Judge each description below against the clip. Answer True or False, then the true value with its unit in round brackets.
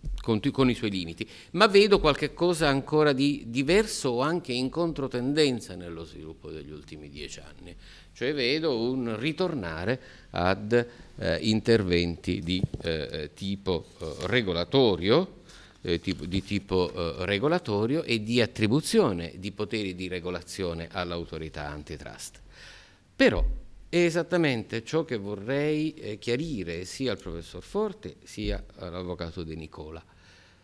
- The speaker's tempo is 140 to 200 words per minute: False (125 wpm)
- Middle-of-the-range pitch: False (105 Hz)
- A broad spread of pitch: True (7.6 semitones)